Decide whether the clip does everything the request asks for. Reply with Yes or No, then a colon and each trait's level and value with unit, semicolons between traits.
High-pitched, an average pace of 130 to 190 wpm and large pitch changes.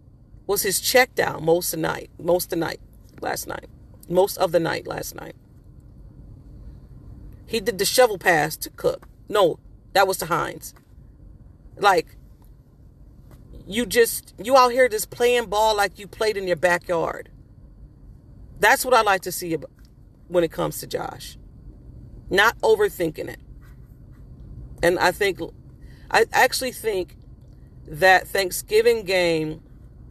Yes: high, 200 Hz; average, 140 wpm; wide, 6.8 semitones